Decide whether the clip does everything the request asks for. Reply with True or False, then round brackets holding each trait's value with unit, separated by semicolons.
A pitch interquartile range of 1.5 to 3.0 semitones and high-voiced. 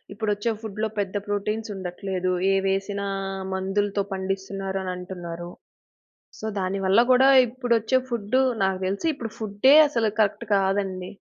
True (2.4 semitones; 200 Hz)